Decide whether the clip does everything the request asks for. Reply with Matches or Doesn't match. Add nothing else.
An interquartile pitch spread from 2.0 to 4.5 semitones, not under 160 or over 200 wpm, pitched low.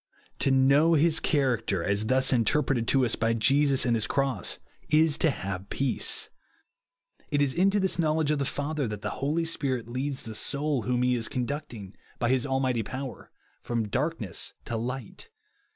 Matches